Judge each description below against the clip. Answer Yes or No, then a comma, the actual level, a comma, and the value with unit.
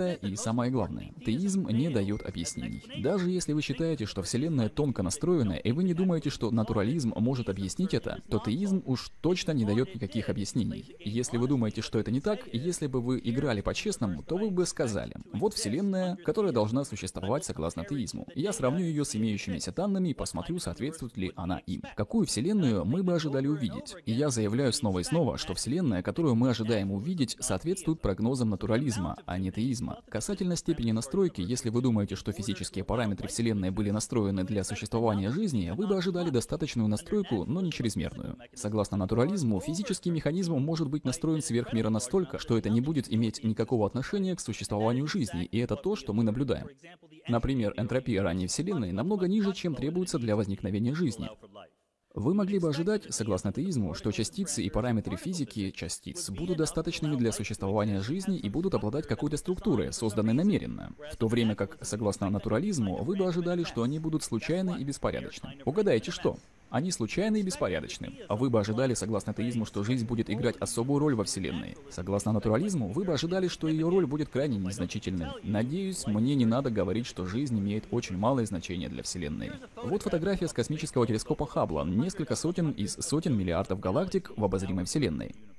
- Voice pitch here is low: Yes, low, 120 Hz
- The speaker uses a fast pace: Yes, fast, 175 wpm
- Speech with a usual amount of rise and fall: No, wide, 7.3 semitones